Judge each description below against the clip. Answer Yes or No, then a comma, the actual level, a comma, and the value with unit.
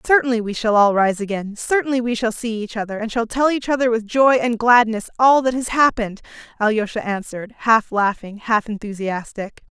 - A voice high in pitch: Yes, high, 225 Hz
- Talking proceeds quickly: No, average, 190 wpm